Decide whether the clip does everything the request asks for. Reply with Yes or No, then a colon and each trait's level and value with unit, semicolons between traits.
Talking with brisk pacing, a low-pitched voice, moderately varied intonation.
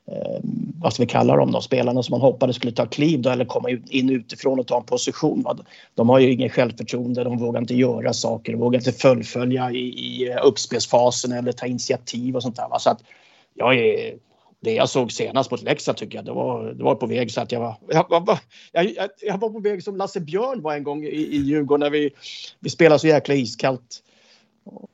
Yes: fast, 220 wpm; low, 130 Hz; average, 3.6 semitones